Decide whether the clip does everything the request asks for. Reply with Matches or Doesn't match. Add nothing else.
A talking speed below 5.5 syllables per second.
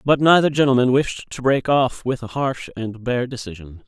Matches